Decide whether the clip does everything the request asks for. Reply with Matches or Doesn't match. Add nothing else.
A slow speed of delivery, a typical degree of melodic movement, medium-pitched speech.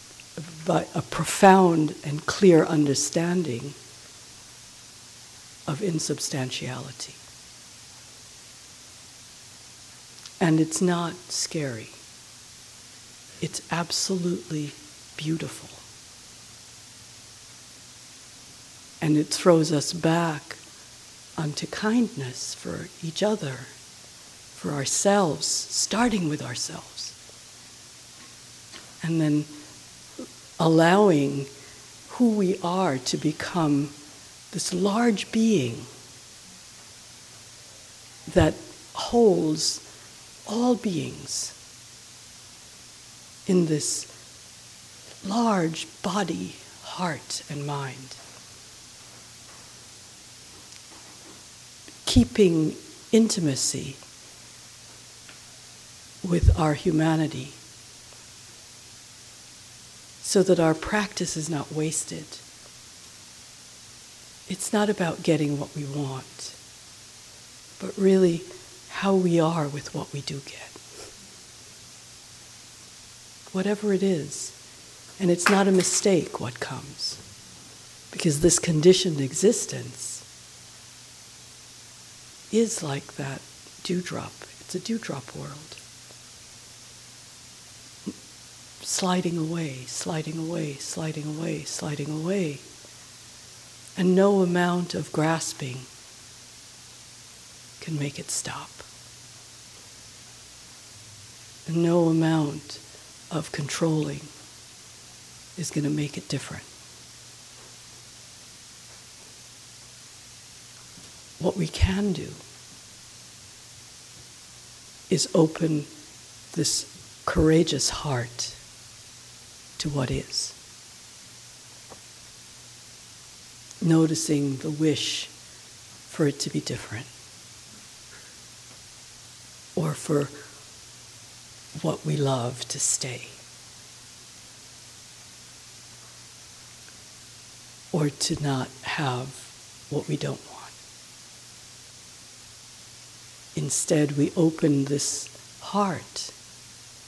Matches